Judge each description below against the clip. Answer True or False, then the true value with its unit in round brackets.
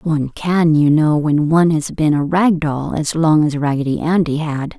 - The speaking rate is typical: False (215 wpm)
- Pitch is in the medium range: True (155 Hz)